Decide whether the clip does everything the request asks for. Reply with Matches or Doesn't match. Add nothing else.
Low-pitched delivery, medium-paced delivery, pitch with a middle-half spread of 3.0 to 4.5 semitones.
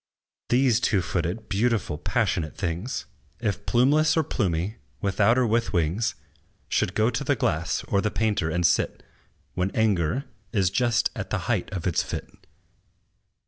Doesn't match